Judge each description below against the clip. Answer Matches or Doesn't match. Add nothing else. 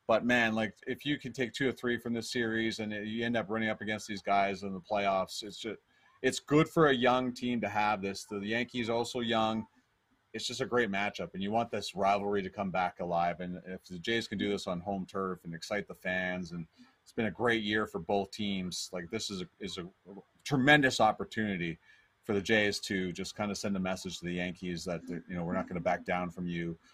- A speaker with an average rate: Doesn't match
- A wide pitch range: Doesn't match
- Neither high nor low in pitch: Doesn't match